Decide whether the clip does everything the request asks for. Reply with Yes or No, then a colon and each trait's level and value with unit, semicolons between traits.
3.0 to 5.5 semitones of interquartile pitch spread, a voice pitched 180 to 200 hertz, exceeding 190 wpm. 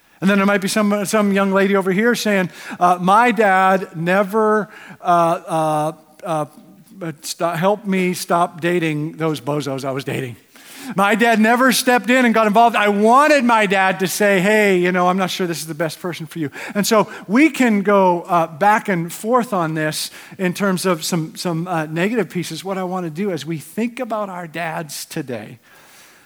Yes: average, 4.0 semitones; high, 190 Hz; average, 200 wpm